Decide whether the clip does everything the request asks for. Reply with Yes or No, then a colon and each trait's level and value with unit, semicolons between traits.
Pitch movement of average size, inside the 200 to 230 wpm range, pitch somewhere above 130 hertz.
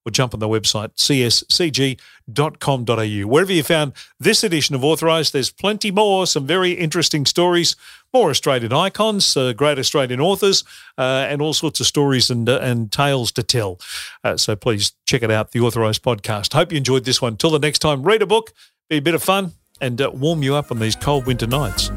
Yes: average, 5.0 semitones; fast, 205 wpm; medium, 140 Hz